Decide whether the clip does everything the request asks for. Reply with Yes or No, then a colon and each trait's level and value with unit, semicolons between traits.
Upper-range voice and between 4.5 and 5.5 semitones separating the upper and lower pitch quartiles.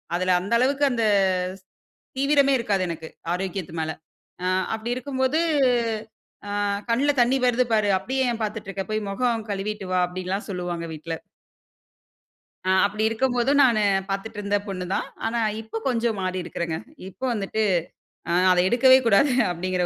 Yes: high, 215 Hz; average, 4.9 semitones